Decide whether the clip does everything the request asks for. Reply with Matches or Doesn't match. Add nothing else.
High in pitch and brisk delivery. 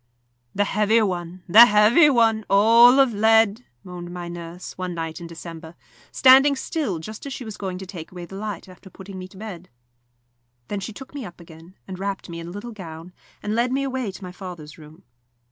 Matches